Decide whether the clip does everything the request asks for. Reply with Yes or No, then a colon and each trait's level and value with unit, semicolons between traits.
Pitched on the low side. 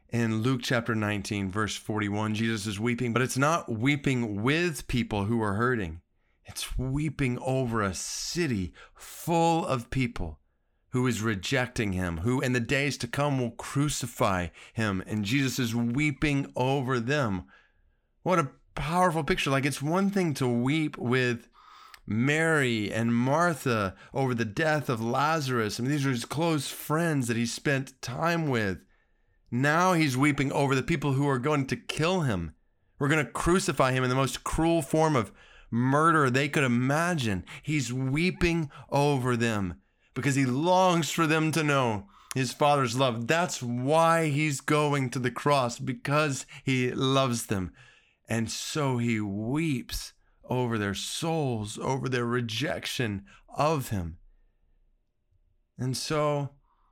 Yes: low, 130 Hz